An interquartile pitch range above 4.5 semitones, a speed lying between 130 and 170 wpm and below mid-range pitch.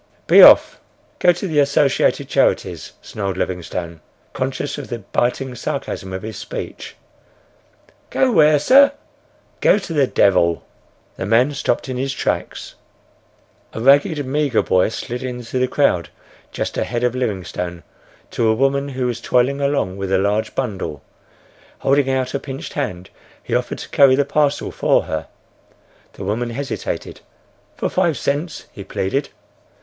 Yes: wide, 5.6 semitones; average, 150 wpm; low, 130 Hz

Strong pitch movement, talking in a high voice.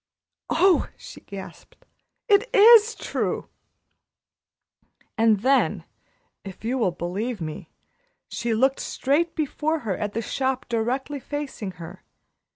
Yes: wide, 6.3 semitones; very high, 250 Hz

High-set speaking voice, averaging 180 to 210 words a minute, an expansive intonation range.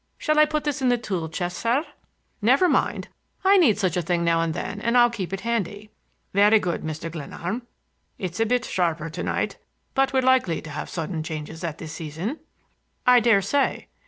Yes: high, 200 Hz; average, 200 wpm; wide, 6.8 semitones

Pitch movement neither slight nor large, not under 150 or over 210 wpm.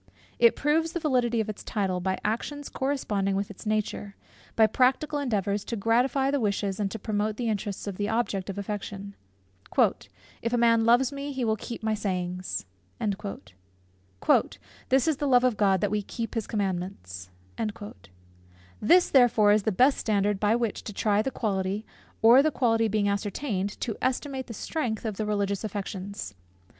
Yes: average, 3.5 semitones; average, 170 wpm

